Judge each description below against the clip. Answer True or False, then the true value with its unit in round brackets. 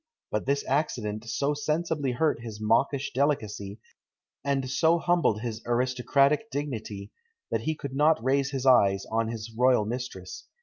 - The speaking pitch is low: True (130 Hz)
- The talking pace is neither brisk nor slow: True (145 wpm)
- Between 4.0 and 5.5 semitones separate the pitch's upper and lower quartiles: True (4.3 semitones)